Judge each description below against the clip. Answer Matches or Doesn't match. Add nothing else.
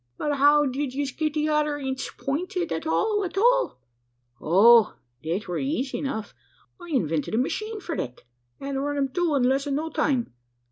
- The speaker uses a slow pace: Doesn't match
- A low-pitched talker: Doesn't match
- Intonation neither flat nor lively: Matches